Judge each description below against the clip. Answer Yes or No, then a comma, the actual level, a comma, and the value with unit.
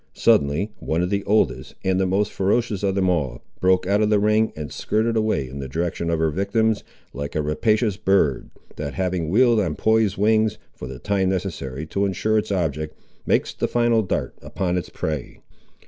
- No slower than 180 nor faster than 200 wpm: Yes, average, 195 wpm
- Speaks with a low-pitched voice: Yes, very low, 95 Hz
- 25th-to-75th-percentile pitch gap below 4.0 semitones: No, average, 5.3 semitones